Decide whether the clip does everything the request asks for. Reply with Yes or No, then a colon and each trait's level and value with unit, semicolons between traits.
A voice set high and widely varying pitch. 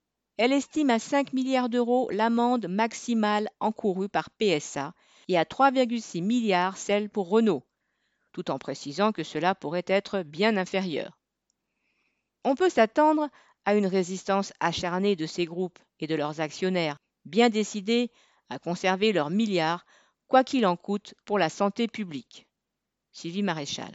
No: high, 205 Hz; average, 4.6 semitones